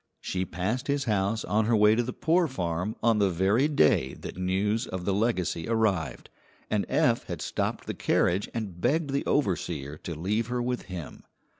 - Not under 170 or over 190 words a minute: Yes, average, 185 wpm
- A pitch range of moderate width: Yes, average, 4.7 semitones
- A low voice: Yes, low, 105 Hz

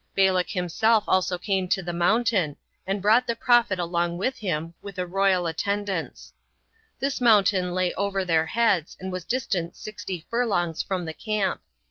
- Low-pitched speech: No, high, 190 Hz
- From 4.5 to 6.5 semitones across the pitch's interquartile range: No, average, 3.3 semitones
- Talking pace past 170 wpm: No, average, 160 wpm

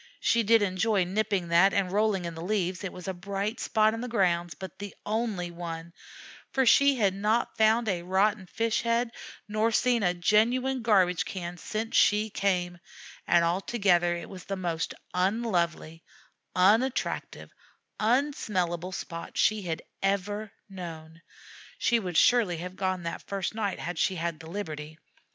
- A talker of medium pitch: No, high, 195 Hz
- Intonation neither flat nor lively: Yes, average, 3.8 semitones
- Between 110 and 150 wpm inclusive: No, average, 160 wpm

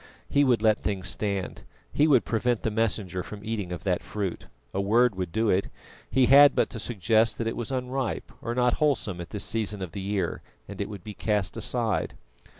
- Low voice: Yes, low, 110 Hz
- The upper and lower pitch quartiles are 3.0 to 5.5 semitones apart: Yes, average, 3.6 semitones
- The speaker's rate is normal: No, fast, 210 wpm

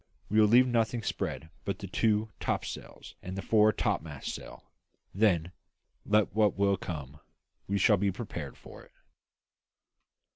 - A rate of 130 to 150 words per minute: Yes, average, 145 wpm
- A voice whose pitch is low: Yes, low, 100 Hz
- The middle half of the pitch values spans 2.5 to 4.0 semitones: Yes, average, 3.4 semitones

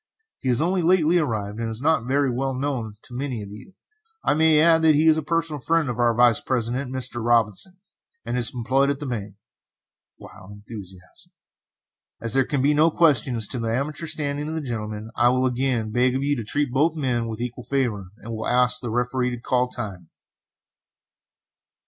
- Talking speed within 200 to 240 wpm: Yes, fast, 205 wpm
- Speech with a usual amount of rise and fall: Yes, average, 4.0 semitones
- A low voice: Yes, low, 125 Hz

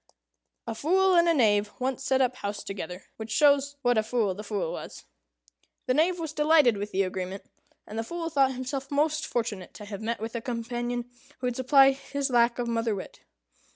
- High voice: Yes, high, 245 Hz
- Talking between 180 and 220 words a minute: Yes, average, 200 wpm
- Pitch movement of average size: Yes, average, 4.5 semitones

